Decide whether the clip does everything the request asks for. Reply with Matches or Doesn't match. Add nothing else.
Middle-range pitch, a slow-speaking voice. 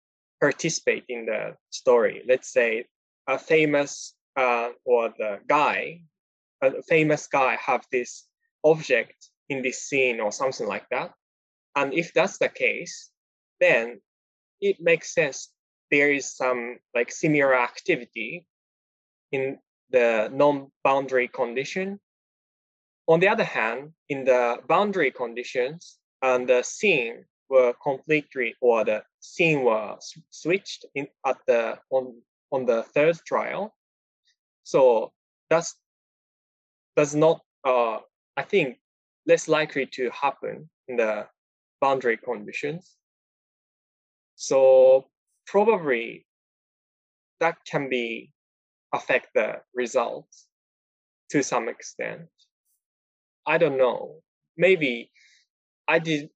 Matches